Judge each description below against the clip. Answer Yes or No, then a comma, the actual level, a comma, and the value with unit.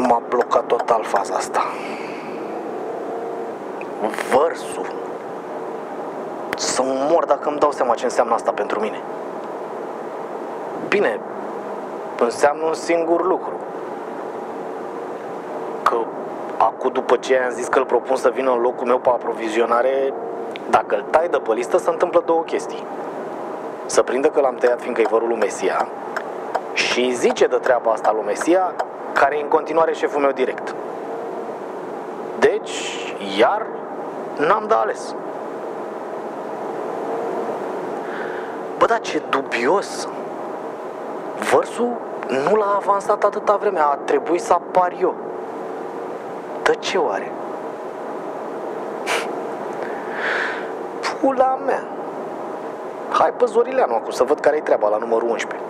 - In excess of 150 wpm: No, slow, 115 wpm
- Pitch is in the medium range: Yes, medium, 165 Hz